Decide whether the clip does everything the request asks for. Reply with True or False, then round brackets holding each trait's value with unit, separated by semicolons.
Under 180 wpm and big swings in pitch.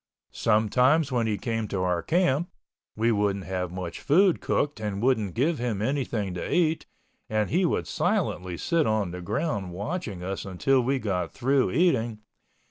True (160 wpm; 6.2 semitones)